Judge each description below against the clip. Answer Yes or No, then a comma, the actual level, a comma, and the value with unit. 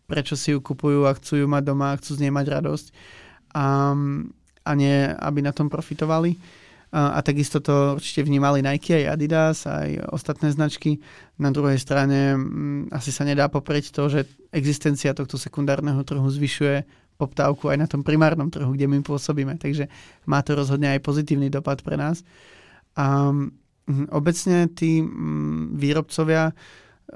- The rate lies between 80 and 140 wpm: No, average, 160 wpm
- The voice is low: No, medium, 145 Hz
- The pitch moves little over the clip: Yes, narrow, 1.3 semitones